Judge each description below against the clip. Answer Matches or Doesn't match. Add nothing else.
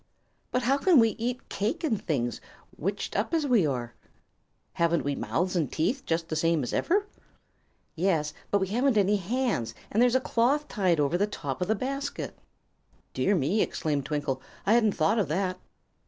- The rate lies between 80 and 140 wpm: Doesn't match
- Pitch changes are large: Matches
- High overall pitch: Matches